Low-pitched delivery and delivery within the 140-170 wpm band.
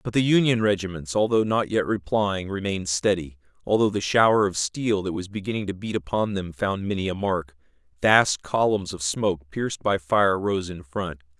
No: very low, 95 Hz; average, 190 wpm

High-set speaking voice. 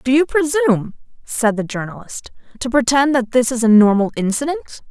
Yes: high, 245 Hz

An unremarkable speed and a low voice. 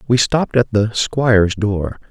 Yes: average, 170 wpm; low, 110 Hz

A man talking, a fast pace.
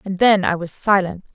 No: female; fast, 225 wpm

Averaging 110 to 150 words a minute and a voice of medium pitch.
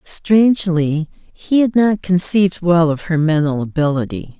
Yes: slow, 135 wpm; medium, 170 Hz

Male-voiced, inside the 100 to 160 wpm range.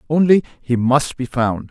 Yes: male; average, 140 wpm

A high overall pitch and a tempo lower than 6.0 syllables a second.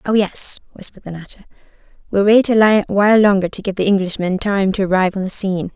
No: high, 195 Hz; 6.3 syllables/s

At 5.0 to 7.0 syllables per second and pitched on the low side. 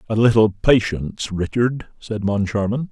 No: 4.6 syllables/s; low, 110 Hz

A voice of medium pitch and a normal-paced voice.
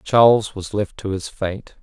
No: low, 100 Hz; average, 195 wpm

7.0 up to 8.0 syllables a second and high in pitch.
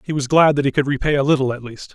No: 7.1 syllables/s; medium, 140 Hz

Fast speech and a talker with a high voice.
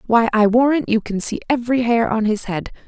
Yes: fast, 230 wpm; high, 230 Hz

